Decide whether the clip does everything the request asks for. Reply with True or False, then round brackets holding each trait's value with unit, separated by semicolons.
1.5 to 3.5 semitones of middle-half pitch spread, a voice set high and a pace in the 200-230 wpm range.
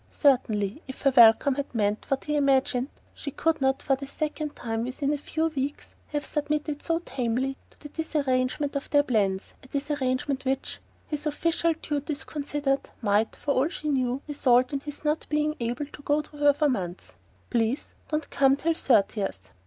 False (2.7 semitones; 280 Hz; 180 wpm)